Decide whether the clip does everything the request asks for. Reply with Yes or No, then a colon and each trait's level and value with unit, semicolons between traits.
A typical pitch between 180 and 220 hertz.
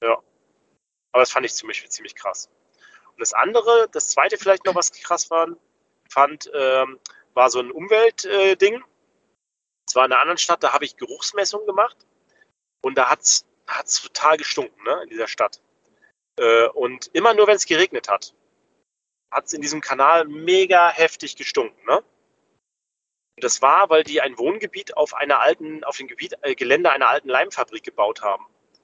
Yes: high, 190 Hz